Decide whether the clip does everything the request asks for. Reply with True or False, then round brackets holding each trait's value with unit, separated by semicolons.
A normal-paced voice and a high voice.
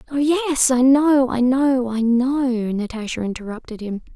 True (160 wpm; 250 Hz)